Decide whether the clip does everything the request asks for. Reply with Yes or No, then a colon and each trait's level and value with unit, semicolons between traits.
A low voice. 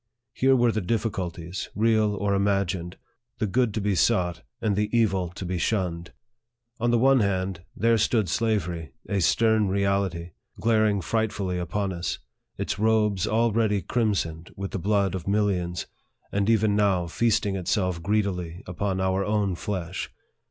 Yes: low, 100 Hz